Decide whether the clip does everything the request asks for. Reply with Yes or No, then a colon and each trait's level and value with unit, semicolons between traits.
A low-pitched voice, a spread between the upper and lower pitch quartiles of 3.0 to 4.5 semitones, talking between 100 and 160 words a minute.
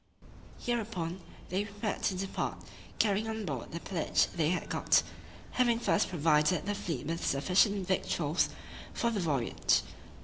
No: medium, 185 Hz; average, 4.0 semitones; average, 145 wpm